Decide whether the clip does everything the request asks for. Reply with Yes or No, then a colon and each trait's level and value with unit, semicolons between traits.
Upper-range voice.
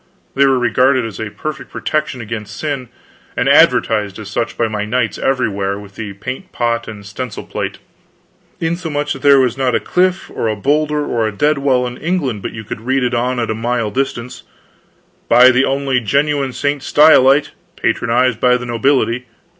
No: low, 125 Hz